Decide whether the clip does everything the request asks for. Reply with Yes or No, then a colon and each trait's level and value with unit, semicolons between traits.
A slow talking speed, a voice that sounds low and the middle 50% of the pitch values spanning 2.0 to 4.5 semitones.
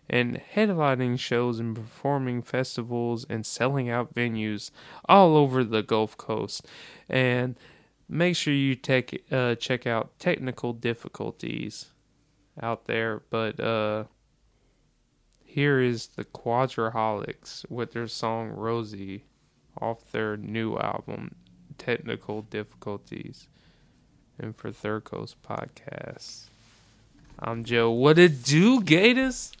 Yes: slow, 110 wpm; low, 120 Hz; average, 2.8 semitones